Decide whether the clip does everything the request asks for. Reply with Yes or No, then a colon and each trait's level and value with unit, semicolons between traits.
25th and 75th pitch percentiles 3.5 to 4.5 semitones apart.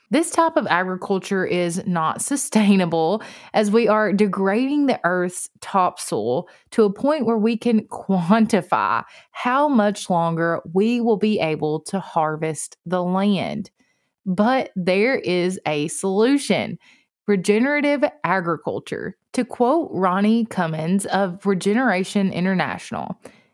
Yes: average, 3.9 semitones